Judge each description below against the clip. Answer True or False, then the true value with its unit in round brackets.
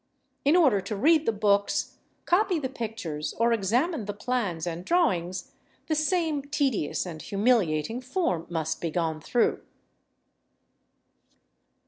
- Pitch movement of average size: False (8.4 semitones)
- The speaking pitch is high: True (220 Hz)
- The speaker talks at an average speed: False (125 wpm)